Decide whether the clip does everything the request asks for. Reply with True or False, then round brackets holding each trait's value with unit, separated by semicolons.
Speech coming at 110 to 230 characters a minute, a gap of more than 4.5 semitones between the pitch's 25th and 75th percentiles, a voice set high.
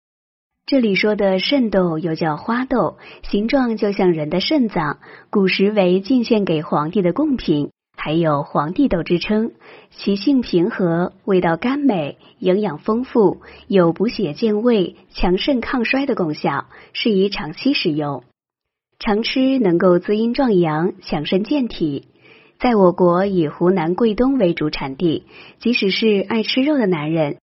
True (215 characters per minute; 5.1 semitones; 195 Hz)